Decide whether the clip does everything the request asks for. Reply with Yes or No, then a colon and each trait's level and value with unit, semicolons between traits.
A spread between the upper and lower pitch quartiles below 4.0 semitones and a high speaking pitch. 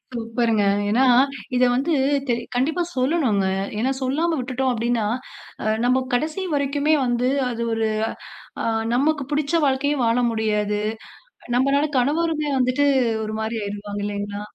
No: average, 4.3 semitones; very high, 250 Hz